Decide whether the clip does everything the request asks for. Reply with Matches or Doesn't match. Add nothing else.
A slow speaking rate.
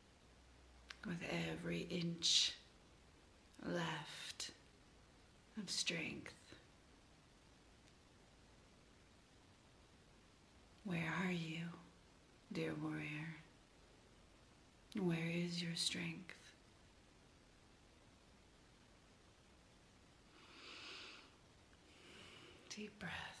Matches